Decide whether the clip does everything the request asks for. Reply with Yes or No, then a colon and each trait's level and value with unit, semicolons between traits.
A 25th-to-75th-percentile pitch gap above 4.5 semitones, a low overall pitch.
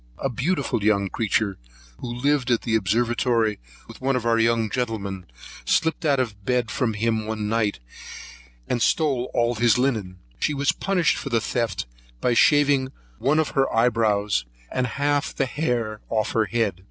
No: average, 3.5 semitones; low, 120 Hz